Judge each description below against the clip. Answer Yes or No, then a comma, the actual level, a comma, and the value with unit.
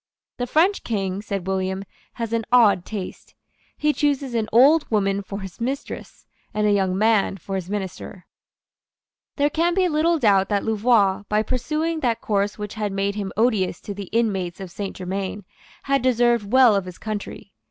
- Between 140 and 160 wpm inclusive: No, average, 175 wpm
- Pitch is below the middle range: No, high, 210 Hz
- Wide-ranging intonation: No, average, 4.1 semitones